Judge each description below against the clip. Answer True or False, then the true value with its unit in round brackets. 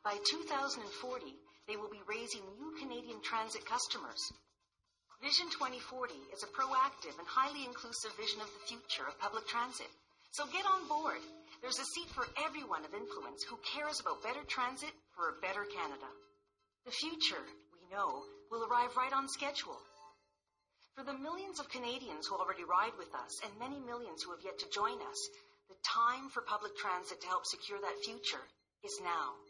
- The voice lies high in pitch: True (245 Hz)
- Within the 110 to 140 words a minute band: False (175 wpm)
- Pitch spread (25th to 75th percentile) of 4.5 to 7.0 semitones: True (5.6 semitones)